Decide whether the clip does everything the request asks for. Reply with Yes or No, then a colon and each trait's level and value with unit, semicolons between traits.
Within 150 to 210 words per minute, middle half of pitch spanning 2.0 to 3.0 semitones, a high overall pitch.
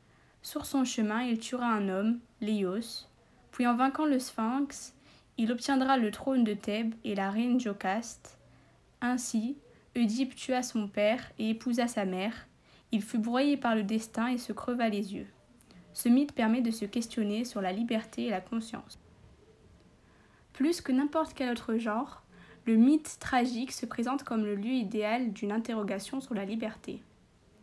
Yes: average, 165 wpm; narrow, 2.6 semitones; high, 230 Hz